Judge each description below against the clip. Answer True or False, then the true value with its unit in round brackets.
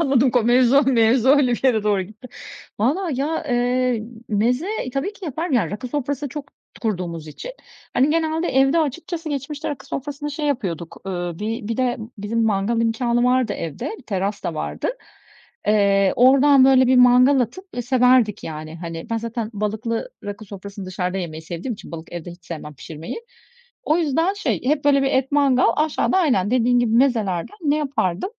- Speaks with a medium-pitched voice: False (245 Hz)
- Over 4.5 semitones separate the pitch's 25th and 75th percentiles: True (5.4 semitones)